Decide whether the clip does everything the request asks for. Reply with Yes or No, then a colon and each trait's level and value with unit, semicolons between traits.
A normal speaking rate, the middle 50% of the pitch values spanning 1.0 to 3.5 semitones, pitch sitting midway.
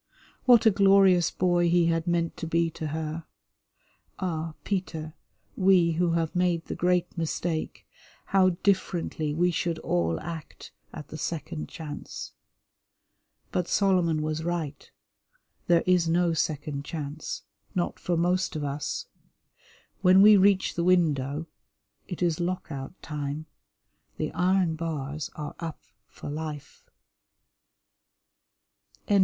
No: slow, 125 wpm; narrow, 2.6 semitones; medium, 170 Hz